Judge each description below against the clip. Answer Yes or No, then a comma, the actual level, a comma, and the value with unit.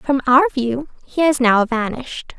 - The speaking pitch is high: Yes, very high, 260 Hz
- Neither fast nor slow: Yes, average, 175 wpm